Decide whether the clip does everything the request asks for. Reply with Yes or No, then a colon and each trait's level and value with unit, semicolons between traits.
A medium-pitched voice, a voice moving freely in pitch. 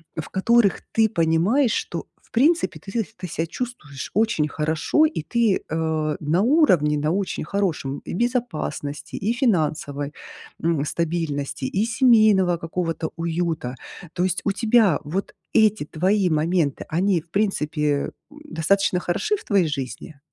Yes: medium, 175 Hz; wide, 5.7 semitones